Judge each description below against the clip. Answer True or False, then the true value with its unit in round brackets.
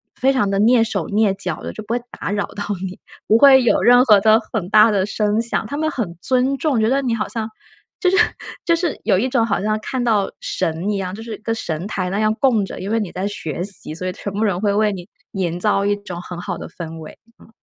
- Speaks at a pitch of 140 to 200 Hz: False (210 Hz)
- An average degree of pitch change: True (3.3 semitones)